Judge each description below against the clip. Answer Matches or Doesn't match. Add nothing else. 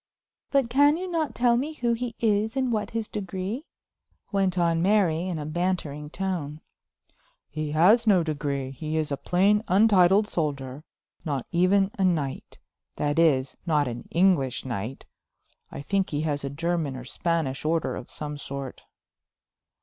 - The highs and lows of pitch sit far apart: Matches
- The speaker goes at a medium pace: Matches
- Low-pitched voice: Doesn't match